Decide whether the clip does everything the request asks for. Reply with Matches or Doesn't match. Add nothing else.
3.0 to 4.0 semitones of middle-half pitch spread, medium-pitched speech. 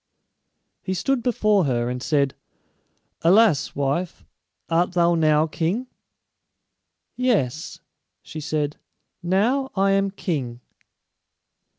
Doesn't match